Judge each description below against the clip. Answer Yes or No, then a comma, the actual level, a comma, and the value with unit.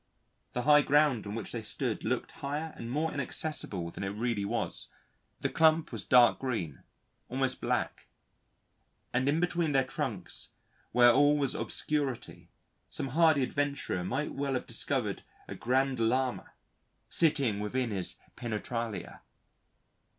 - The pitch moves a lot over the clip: No, average, 3.9 semitones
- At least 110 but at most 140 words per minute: Yes, slow, 135 wpm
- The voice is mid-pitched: No, low, 130 Hz